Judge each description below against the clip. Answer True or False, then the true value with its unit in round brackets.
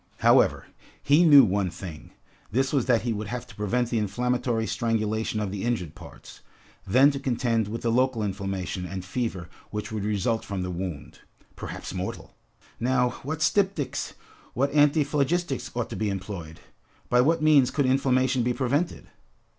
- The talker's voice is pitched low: True (120 Hz)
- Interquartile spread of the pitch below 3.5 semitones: False (4.6 semitones)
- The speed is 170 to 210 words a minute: False (160 wpm)